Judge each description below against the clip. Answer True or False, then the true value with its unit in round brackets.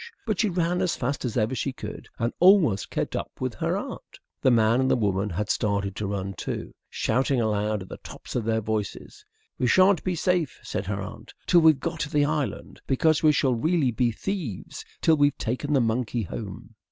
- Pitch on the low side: True (125 Hz)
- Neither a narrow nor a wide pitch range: False (6.6 semitones)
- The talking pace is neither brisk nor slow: False (210 wpm)